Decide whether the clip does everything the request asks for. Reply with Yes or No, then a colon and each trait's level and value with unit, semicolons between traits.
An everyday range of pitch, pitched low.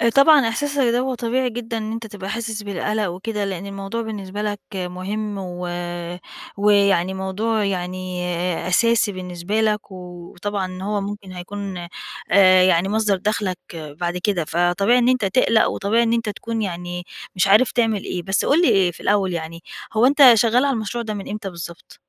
No: average, 3.5 semitones; high, 200 Hz